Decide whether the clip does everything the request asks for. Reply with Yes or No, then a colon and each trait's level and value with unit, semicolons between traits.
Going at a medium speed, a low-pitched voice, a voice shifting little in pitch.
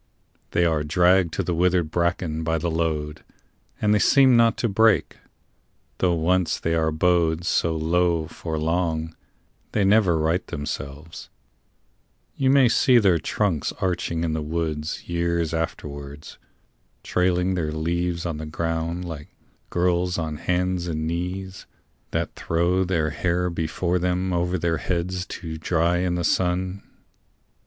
Yes: average, 145 wpm; very low, 85 Hz; narrow, 2.1 semitones